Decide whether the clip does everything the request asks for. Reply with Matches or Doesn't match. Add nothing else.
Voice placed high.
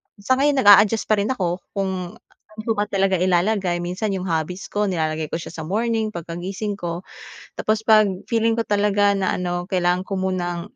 Matches